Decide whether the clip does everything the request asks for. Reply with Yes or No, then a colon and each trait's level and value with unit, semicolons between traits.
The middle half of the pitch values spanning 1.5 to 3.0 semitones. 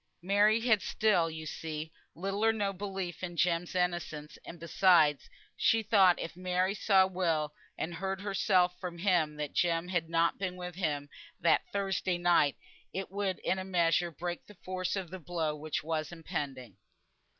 Yes: average, 2.7 semitones